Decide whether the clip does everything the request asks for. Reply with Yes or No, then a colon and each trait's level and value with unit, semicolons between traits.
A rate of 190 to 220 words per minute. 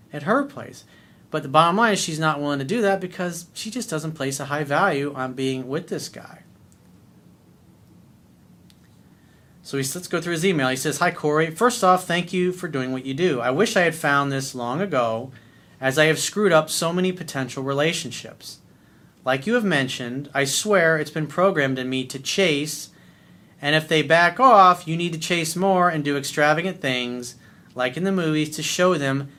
Yes: average, 200 wpm